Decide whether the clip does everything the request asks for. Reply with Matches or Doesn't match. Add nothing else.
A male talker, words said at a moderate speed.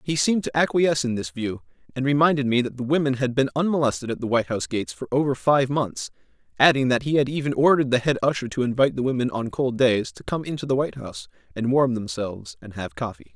Doesn't match